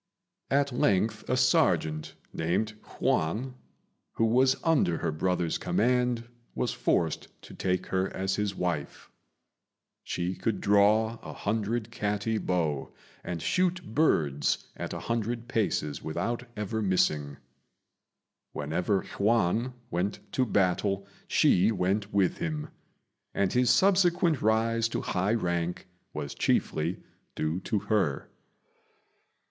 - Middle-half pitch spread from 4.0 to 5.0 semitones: Yes, average, 4.7 semitones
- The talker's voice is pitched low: Yes, low, 105 Hz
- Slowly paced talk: Yes, slow, 120 wpm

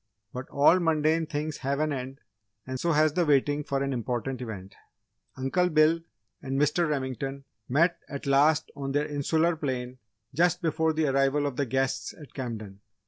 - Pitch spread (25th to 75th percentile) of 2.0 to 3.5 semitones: Yes, average, 2.9 semitones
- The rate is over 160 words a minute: Yes, average, 170 wpm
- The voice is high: No, medium, 140 Hz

